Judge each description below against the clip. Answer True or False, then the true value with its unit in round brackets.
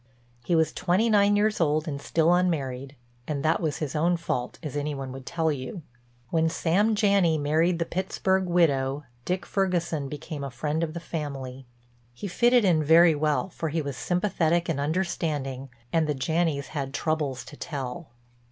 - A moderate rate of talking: True (175 wpm)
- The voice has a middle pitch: True (160 Hz)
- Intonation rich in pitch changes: False (3.5 semitones)